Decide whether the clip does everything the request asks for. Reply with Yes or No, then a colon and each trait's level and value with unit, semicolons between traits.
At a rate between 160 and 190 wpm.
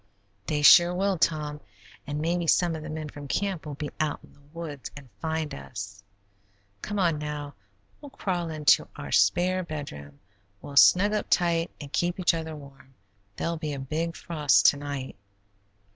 Yes: average, 175 wpm